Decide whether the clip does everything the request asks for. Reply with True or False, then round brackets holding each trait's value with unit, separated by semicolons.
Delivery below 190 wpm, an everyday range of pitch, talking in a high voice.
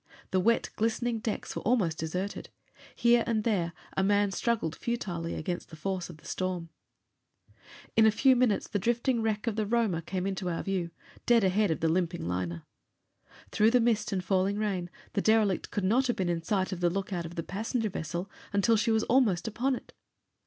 False (195 wpm; 4.2 semitones; 200 Hz)